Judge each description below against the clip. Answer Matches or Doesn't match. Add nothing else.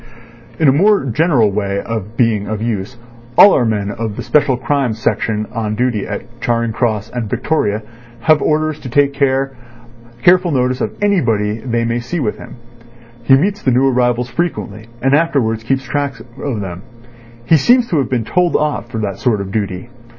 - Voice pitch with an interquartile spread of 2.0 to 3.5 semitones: Doesn't match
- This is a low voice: Matches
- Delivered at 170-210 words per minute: Matches